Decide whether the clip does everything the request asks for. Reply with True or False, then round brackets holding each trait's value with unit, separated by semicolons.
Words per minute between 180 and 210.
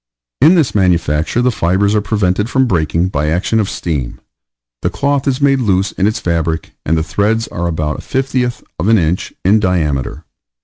True (185 wpm)